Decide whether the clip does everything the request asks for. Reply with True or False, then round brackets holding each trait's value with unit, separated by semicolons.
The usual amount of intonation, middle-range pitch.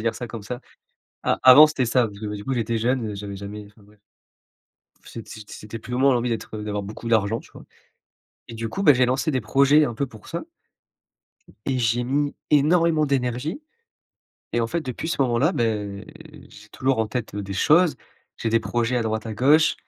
False (3.8 semitones; 120 Hz)